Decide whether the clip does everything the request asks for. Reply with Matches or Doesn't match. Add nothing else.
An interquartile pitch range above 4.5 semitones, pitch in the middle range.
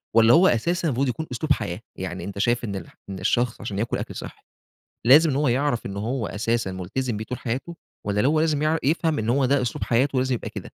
Doesn't match